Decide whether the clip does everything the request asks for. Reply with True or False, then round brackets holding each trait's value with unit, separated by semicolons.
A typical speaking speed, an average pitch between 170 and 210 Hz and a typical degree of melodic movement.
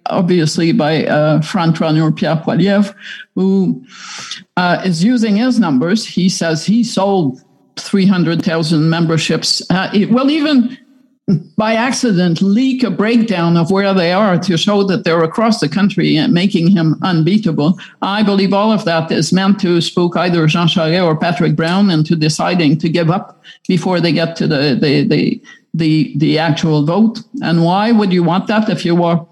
True (170 wpm; 185 Hz; 4.1 semitones)